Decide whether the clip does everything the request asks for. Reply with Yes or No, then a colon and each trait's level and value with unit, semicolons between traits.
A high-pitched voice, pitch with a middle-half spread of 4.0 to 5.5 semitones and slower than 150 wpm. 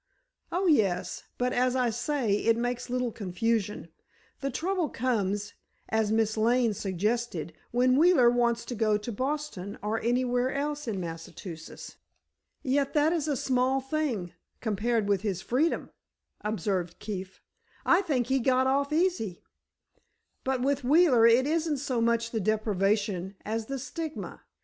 Yes: high, 240 Hz; average, 4.4 semitones; average, 140 wpm